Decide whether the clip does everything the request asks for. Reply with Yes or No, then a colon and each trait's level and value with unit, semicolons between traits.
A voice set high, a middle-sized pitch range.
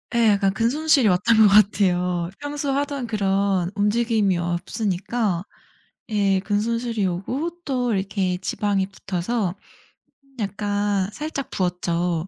Yes: high, 205 Hz; average, 3.8 semitones